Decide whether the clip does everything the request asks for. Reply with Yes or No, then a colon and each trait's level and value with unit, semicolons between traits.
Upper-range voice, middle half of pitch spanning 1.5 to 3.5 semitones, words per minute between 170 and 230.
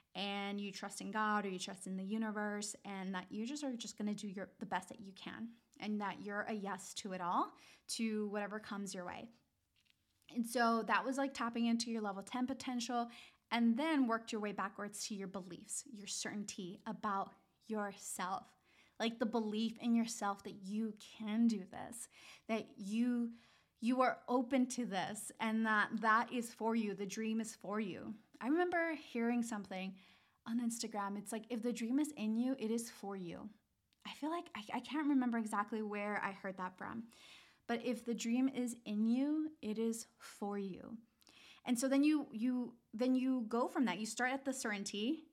Yes: high, 225 Hz; average, 3.1 semitones; average, 195 wpm